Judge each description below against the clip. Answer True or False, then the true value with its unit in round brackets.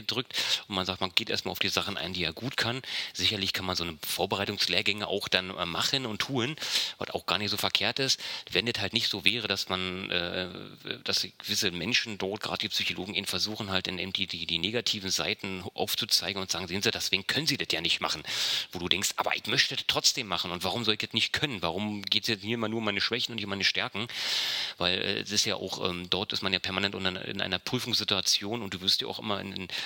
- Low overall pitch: True (100 Hz)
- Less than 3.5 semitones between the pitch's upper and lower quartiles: True (3.0 semitones)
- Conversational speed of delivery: False (245 wpm)